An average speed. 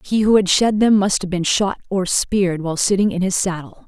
No: fast, 245 wpm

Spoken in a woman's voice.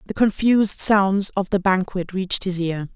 Yes: female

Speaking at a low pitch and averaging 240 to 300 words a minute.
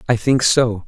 No: low, 120 Hz; fast, 205 wpm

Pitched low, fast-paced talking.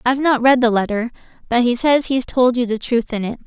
No: high, 245 Hz; fast, 260 wpm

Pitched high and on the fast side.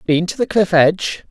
No: medium, 175 Hz; fast, 230 wpm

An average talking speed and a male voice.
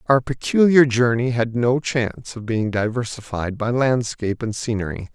Yes: average, 150 wpm; male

